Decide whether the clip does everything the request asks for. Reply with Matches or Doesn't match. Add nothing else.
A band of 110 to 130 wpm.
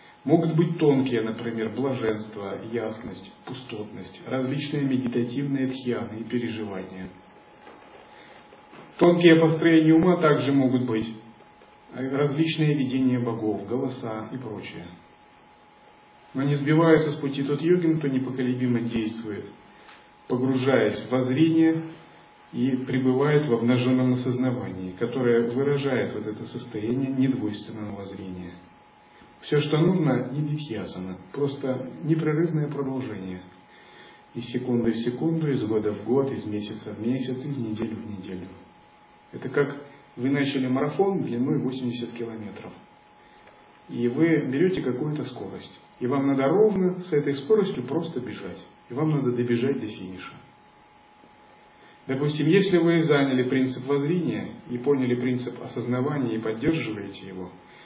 Matches